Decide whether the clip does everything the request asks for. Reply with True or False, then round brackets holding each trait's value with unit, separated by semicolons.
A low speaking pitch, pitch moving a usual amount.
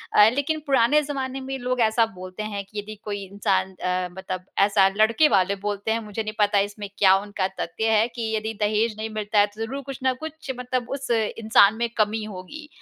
False (215 Hz; 3.5 semitones)